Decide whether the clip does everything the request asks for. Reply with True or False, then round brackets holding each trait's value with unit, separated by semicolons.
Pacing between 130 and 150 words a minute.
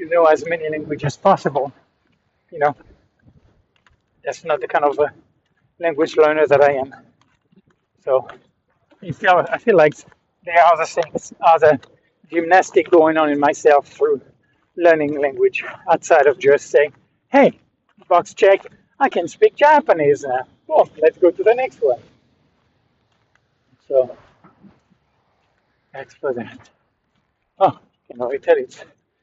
True (140 wpm)